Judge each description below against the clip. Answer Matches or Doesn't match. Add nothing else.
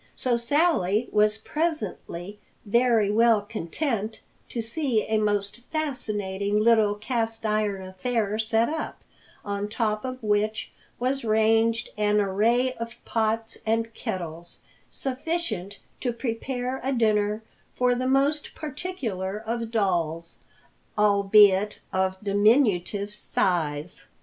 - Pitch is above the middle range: Matches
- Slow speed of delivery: Matches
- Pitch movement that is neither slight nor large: Matches